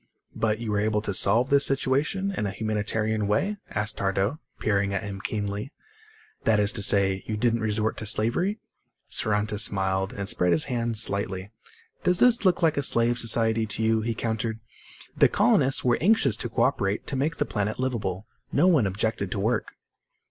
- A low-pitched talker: Yes, low, 110 Hz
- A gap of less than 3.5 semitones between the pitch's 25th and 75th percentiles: Yes, average, 3.1 semitones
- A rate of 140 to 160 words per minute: No, average, 185 wpm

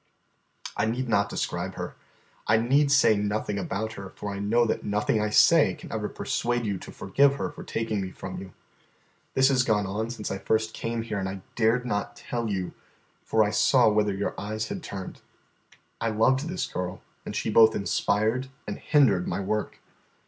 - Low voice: Yes, low, 110 Hz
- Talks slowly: No, average, 190 wpm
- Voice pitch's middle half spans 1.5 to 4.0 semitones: Yes, average, 2.7 semitones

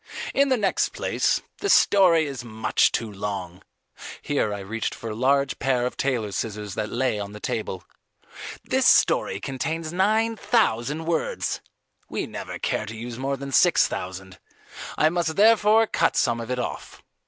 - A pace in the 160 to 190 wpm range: Yes, average, 165 wpm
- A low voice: Yes, low, 125 Hz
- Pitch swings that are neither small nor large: No, wide, 7.2 semitones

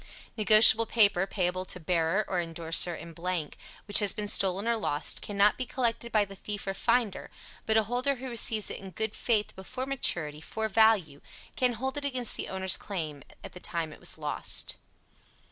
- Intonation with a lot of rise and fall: No, average, 4.2 semitones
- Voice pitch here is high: Yes, high, 205 Hz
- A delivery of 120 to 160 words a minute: No, average, 190 wpm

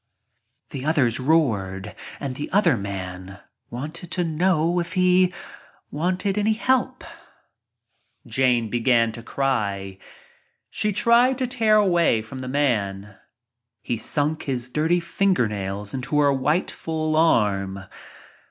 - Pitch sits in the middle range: Yes, medium, 145 Hz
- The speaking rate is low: Yes, slow, 120 wpm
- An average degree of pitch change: No, wide, 7.9 semitones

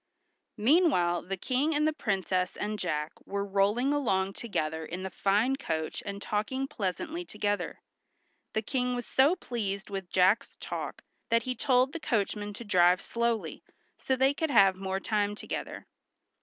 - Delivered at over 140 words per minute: Yes, average, 160 wpm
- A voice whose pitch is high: Yes, high, 210 Hz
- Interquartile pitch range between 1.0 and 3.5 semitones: No, average, 5.2 semitones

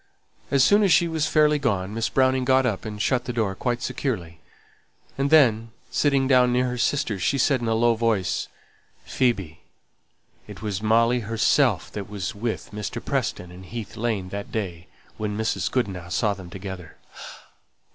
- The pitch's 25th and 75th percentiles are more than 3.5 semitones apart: Yes, average, 4.5 semitones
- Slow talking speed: No, average, 170 wpm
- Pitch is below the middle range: Yes, low, 115 Hz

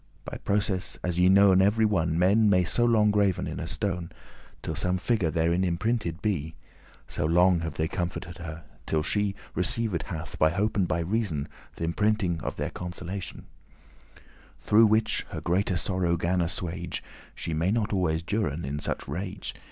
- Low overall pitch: Yes, very low, 90 Hz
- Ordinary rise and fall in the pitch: Yes, average, 3.5 semitones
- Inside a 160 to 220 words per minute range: Yes, average, 170 wpm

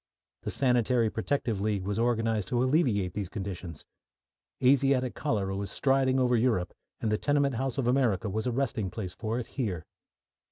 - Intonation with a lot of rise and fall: No, average, 4.2 semitones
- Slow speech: No, average, 165 wpm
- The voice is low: Yes, low, 115 Hz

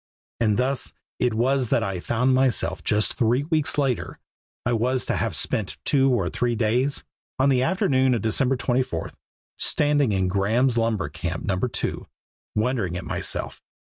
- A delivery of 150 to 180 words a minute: Yes, average, 160 wpm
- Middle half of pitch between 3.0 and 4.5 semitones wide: Yes, average, 3.5 semitones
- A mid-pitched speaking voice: No, low, 125 Hz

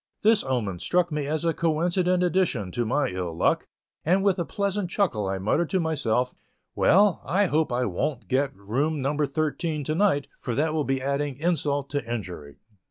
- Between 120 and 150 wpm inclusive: No, average, 185 wpm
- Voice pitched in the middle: Yes, medium, 150 Hz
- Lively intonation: Yes, wide, 5.7 semitones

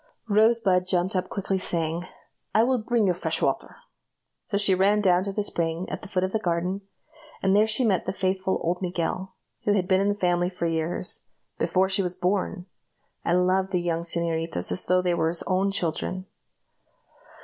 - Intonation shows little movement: Yes, narrow, 2.2 semitones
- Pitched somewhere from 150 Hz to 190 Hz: Yes, medium, 185 Hz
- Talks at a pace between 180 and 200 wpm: Yes, average, 195 wpm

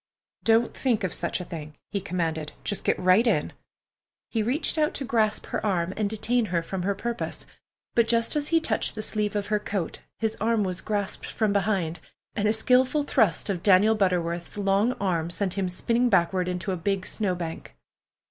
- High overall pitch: Yes, high, 200 Hz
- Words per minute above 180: Yes, average, 190 wpm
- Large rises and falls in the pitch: No, average, 3.7 semitones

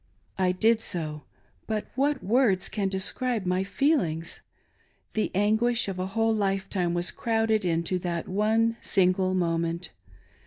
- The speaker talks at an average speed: No, slow, 130 wpm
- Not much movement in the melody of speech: No, average, 3.7 semitones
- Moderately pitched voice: No, high, 195 Hz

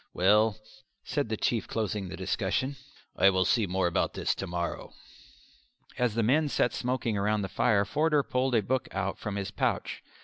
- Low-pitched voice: Yes, low, 105 Hz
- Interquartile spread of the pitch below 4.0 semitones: No, average, 4.3 semitones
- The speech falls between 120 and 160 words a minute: No, average, 180 wpm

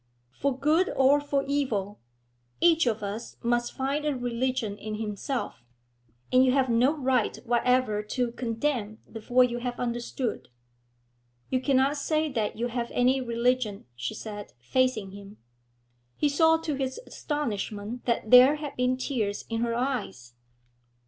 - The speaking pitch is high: Yes, very high, 250 Hz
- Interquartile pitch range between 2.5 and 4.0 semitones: Yes, average, 3.5 semitones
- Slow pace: No, average, 145 wpm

